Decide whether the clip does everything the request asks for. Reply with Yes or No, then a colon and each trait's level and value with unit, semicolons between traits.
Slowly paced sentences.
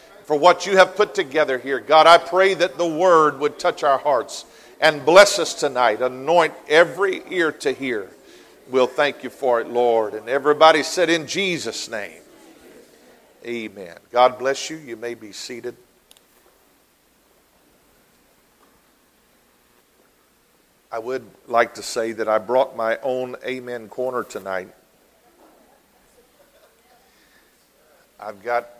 Yes: slow, 125 wpm